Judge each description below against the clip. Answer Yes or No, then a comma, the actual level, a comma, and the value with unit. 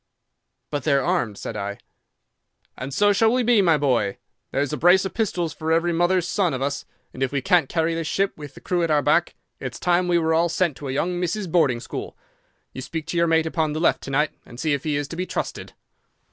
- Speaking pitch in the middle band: Yes, medium, 160 Hz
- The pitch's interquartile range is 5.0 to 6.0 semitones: No, average, 3.9 semitones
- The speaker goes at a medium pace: No, fast, 245 wpm